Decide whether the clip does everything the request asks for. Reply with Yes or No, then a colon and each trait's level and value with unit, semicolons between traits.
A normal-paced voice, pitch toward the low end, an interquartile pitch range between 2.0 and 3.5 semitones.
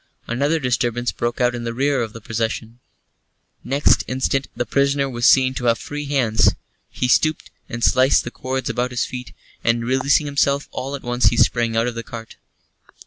Yes: average, 190 wpm; low, 125 Hz; narrow, 2.6 semitones